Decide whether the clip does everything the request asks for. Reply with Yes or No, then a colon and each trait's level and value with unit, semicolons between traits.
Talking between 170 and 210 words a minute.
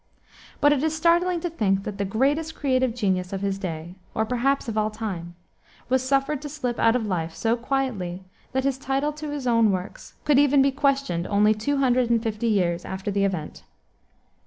Yes: average, 200 wpm